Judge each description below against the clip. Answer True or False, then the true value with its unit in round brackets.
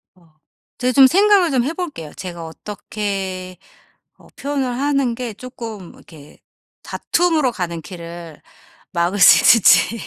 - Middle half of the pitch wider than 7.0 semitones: True (7.6 semitones)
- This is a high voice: True (210 Hz)